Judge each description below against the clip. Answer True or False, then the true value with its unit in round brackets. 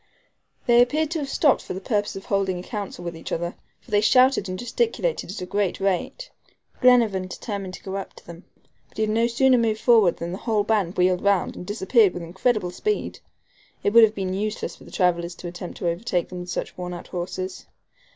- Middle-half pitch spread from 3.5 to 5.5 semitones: True (4.3 semitones)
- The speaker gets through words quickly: True (220 wpm)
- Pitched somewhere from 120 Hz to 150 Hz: False (195 Hz)